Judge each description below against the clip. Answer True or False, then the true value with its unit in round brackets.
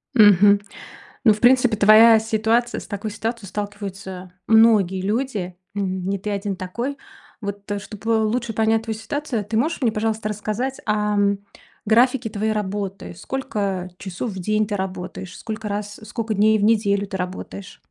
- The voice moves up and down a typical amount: False (2.0 semitones)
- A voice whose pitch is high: True (210 Hz)